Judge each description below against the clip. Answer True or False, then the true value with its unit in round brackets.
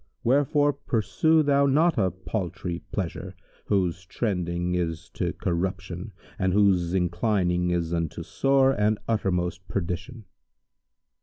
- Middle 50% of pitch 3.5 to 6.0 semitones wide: True (4.7 semitones)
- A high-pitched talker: False (95 Hz)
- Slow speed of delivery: True (110 wpm)